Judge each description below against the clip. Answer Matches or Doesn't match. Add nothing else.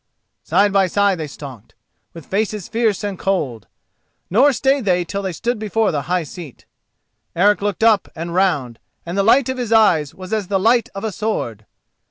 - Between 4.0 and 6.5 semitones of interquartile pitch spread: Matches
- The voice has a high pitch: Matches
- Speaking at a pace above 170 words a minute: Matches